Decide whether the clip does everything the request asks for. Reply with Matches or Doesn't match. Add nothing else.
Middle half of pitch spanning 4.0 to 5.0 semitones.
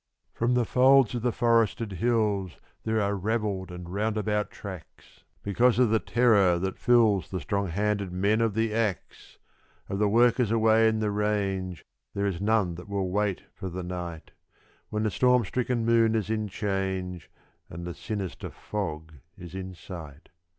Doesn't match